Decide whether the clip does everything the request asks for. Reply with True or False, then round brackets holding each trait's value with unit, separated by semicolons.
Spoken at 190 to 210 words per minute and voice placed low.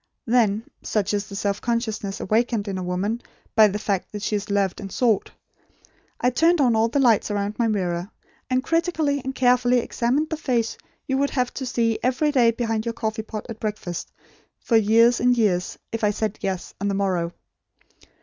False (195 wpm; 225 Hz)